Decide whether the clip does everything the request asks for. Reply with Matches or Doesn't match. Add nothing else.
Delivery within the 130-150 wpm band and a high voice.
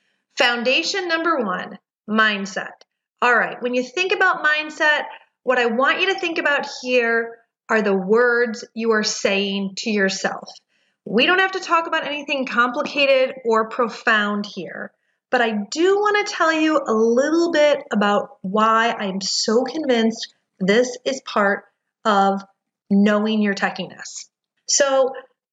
Matches